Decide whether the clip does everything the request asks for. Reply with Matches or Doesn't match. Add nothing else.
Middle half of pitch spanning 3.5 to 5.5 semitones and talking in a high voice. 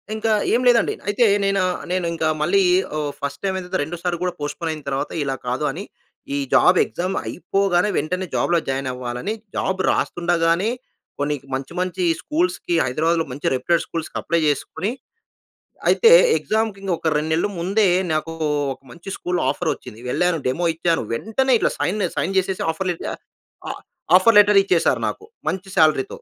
Doesn't match